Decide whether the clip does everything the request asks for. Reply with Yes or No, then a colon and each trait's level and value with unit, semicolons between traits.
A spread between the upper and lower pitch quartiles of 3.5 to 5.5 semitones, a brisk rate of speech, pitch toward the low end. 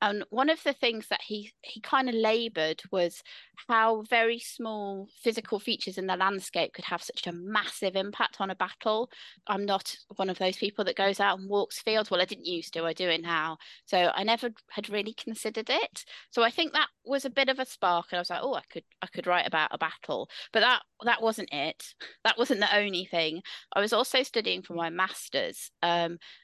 No: average, 3.9 semitones; fast, 220 wpm; high, 205 Hz